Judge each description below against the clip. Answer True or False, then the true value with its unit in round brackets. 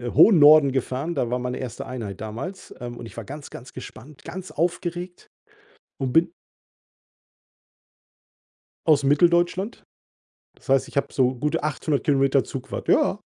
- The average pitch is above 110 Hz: True (140 Hz)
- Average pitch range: True (4.6 semitones)